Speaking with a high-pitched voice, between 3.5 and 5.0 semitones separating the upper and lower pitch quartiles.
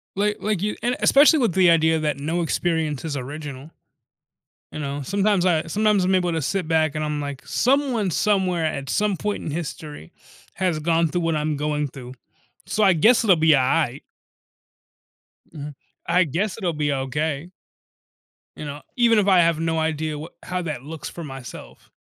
No: medium, 160 Hz; average, 4.1 semitones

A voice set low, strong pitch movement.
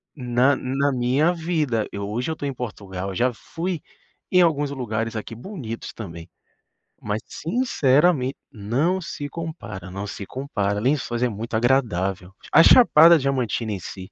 Yes: low, 125 Hz; wide, 6.1 semitones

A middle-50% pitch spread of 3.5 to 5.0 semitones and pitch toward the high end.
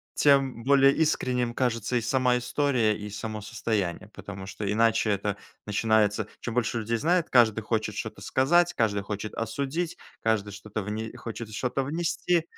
No: average, 3.8 semitones; low, 115 Hz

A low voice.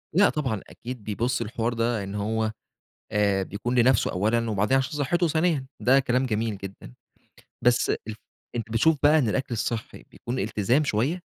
Yes: low, 120 Hz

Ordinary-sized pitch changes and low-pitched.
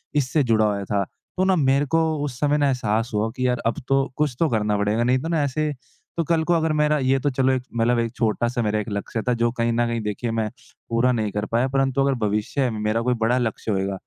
Yes: average, 3.9 semitones; low, 120 Hz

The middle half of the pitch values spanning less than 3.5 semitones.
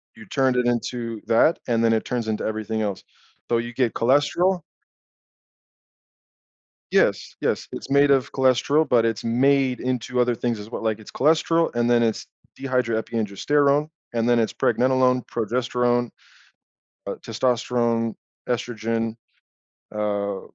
Yes: narrow, 2.4 semitones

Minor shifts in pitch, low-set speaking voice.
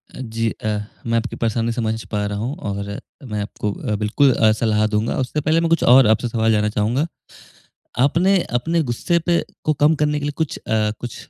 No: wide, 5.4 semitones; low, 115 Hz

